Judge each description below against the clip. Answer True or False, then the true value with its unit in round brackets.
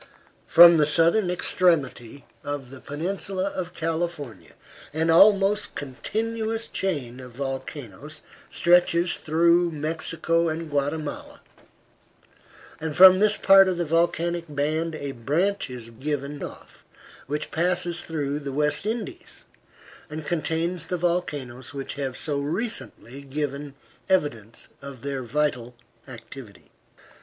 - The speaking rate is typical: False (115 wpm)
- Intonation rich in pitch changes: False (3.9 semitones)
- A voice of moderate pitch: True (155 Hz)